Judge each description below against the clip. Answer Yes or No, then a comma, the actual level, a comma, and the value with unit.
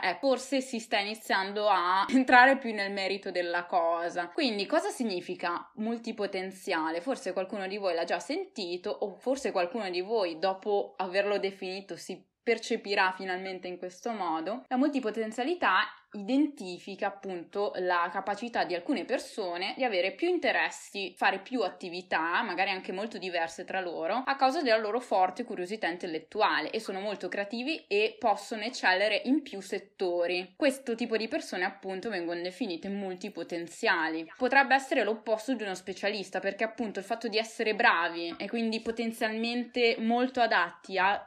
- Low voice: No, high, 205 Hz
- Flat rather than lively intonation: No, average, 4.3 semitones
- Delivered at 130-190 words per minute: Yes, average, 150 wpm